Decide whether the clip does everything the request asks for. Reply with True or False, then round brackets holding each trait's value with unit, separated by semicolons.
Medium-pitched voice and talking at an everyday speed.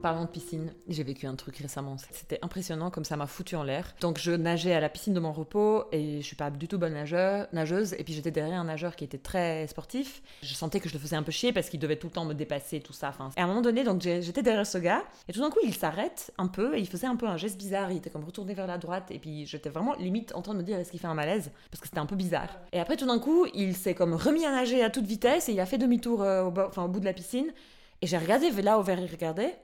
False (175 Hz; 310 wpm)